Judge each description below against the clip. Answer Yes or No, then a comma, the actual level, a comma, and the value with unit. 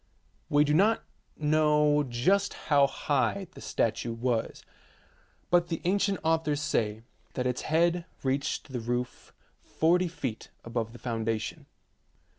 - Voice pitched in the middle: Yes, medium, 145 Hz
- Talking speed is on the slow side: Yes, slow, 125 wpm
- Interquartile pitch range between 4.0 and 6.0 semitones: Yes, average, 5.3 semitones